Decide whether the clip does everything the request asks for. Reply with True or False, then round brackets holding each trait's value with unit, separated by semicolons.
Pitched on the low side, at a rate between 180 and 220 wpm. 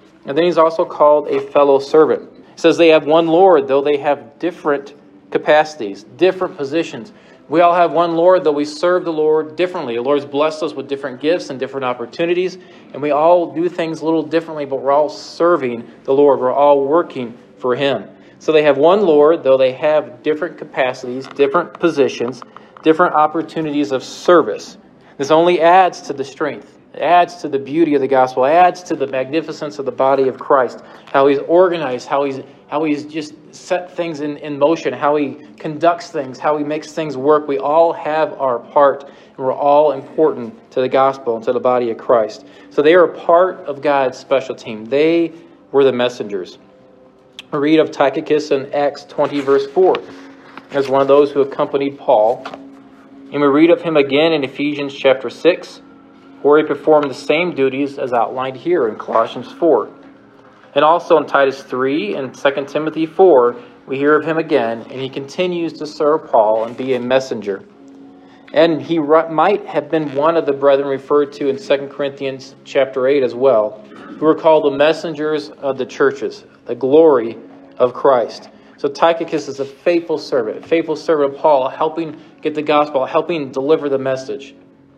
False (145 Hz; 185 wpm)